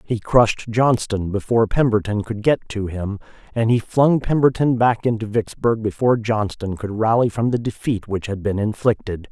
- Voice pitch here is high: No, low, 110 Hz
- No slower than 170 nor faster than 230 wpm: Yes, average, 175 wpm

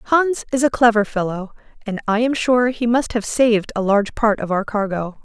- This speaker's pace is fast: Yes, fast, 220 wpm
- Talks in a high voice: Yes, high, 225 Hz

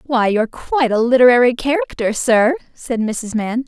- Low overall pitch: No, high, 240 Hz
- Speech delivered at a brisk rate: No, average, 165 wpm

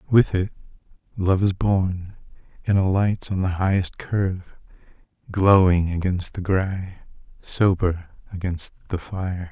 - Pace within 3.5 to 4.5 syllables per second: Yes, 4.1 syllables/s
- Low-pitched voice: Yes, very low, 95 Hz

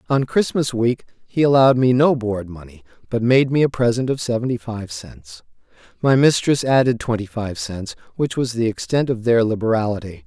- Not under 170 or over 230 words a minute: Yes, average, 180 wpm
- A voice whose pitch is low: Yes, low, 120 Hz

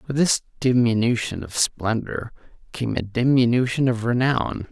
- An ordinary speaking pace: No, slow, 125 wpm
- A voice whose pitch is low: Yes, low, 120 Hz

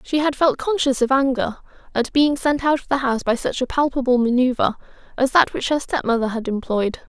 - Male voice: No, female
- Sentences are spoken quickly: Yes, fast, 210 wpm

